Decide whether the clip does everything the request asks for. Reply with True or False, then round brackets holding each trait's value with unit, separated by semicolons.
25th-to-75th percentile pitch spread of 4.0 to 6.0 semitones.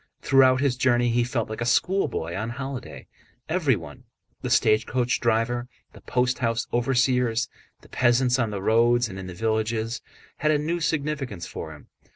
False (2.6 semitones)